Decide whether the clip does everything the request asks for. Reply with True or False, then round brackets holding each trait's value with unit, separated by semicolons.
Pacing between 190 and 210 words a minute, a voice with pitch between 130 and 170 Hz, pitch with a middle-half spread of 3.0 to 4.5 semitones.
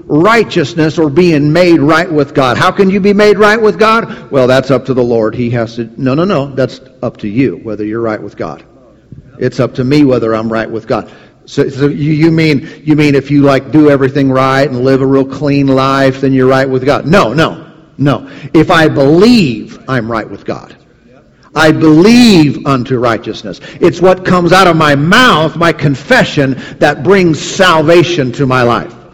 True (200 wpm; 140 Hz; 4.1 semitones)